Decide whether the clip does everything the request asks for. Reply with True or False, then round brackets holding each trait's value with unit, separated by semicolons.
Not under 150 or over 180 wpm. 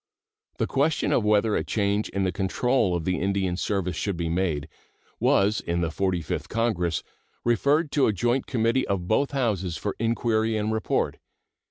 True (170 wpm)